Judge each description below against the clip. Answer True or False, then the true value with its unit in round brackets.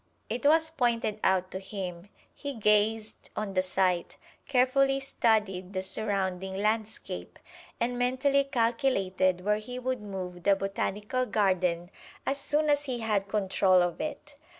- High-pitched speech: True (210 Hz)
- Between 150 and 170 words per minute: False (140 wpm)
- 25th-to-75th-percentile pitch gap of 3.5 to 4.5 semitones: False (5.0 semitones)